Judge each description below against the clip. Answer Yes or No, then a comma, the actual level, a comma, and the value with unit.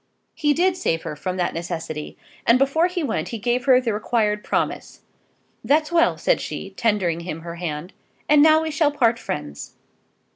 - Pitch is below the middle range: No, high, 230 Hz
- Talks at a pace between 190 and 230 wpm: No, average, 180 wpm